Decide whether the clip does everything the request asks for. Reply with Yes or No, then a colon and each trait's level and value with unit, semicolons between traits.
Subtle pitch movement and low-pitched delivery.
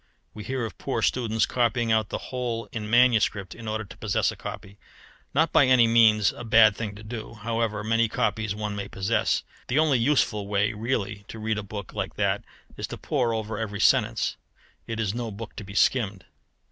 Yes: narrow, 2.0 semitones; low, 110 Hz